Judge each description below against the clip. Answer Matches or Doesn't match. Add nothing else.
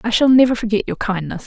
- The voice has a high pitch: Matches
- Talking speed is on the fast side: Matches